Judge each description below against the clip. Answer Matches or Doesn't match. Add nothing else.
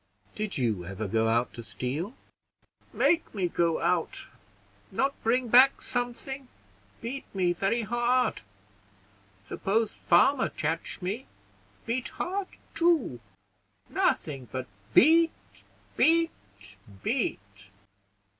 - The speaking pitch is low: Doesn't match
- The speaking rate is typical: Doesn't match